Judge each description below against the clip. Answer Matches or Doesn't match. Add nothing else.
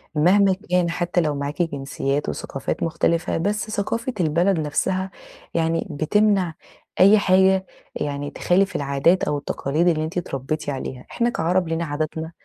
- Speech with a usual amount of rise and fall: Matches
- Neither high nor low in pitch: Matches